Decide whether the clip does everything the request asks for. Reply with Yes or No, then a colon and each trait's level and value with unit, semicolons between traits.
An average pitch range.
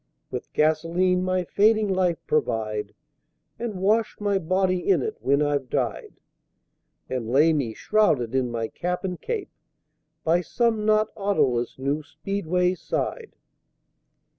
No: wide, 6.2 semitones